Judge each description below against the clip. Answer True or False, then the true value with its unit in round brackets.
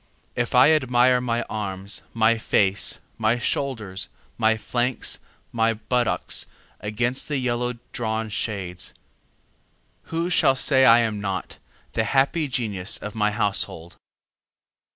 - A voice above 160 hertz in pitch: False (115 Hz)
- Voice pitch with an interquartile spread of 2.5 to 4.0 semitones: True (3.1 semitones)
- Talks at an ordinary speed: False (110 wpm)